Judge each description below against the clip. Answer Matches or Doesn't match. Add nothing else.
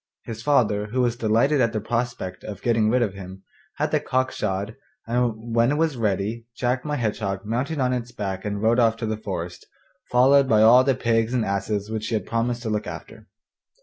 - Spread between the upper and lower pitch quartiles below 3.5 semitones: Matches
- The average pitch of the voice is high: Doesn't match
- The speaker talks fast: Matches